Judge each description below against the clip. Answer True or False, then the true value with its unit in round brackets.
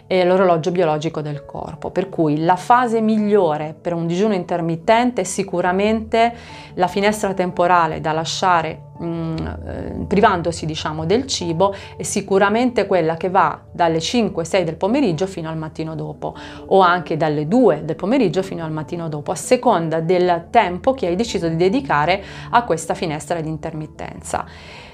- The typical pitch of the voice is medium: True (175 Hz)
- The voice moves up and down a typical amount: True (3.5 semitones)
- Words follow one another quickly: False (155 wpm)